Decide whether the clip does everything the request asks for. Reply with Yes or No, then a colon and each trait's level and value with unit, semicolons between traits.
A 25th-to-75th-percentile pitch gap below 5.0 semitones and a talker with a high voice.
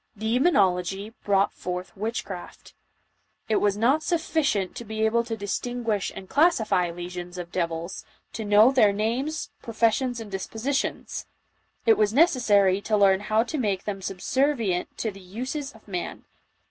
Yes: average, 4.1 semitones; high, 215 Hz